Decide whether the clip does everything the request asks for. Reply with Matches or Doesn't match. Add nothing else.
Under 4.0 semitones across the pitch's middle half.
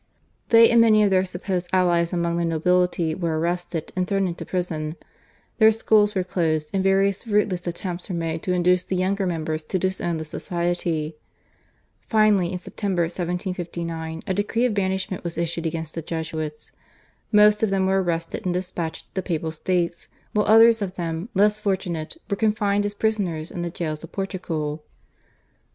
Matches